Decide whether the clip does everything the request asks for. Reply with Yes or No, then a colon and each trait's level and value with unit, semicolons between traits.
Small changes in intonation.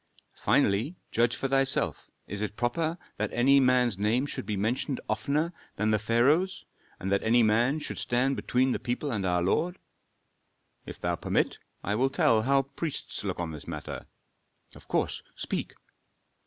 No: average, 4.3 semitones